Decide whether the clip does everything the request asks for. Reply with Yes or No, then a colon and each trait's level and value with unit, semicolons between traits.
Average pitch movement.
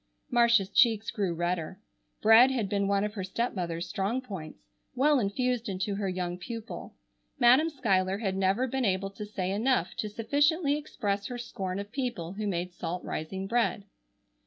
Yes: average, 4.3 semitones